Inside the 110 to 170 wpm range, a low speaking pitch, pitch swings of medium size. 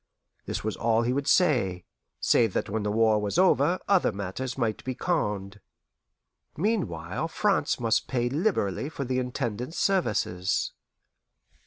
No: average, 140 wpm; low, 120 Hz; wide, 5.9 semitones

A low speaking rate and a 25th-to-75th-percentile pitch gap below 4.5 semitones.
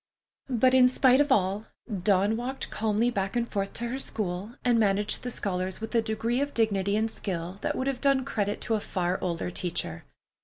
No: average, 200 wpm; average, 4.0 semitones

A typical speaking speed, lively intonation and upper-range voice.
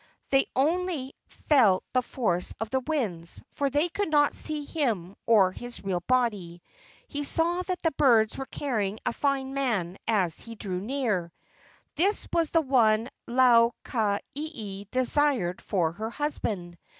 Yes: average, 150 wpm; wide, 6.3 semitones; high, 245 Hz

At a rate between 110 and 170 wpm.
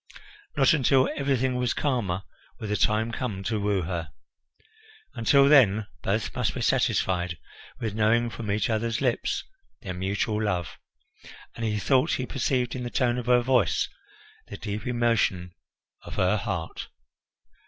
Yes: average, 150 wpm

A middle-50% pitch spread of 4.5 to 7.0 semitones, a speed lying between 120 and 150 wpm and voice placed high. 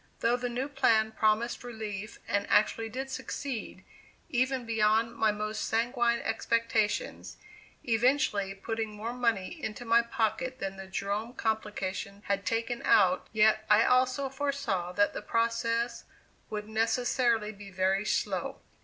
No: narrow, 2.5 semitones; slow, 135 wpm; high, 225 Hz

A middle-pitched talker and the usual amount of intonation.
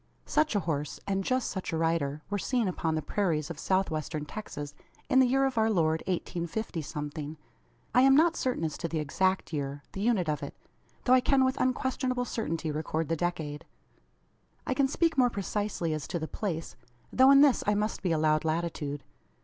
No: medium, 175 Hz; wide, 7.8 semitones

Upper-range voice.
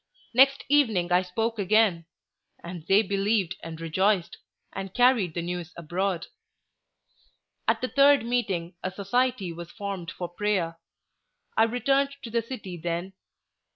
Yes: high, 195 Hz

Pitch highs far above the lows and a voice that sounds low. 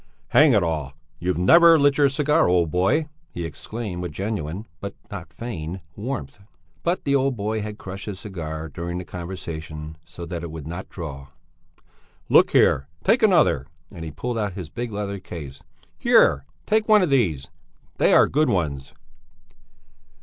Yes: wide, 7.1 semitones; very low, 90 Hz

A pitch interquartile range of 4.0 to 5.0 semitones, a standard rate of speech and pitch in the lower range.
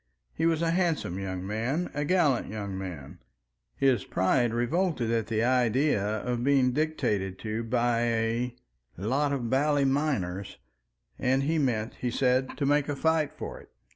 Yes: average, 4.6 semitones; average, 160 wpm; low, 125 Hz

